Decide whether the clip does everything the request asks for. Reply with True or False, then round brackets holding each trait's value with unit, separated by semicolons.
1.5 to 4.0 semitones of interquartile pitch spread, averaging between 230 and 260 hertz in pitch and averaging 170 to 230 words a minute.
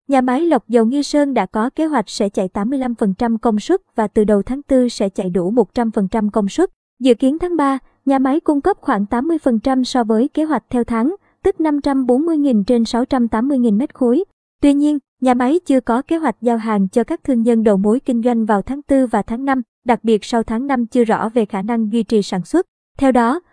True (3.6 semitones; 245 Hz; 225 wpm)